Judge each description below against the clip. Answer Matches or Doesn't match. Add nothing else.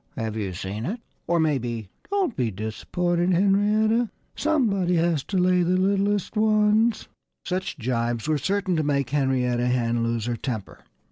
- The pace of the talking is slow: Doesn't match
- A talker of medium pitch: Matches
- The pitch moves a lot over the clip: Matches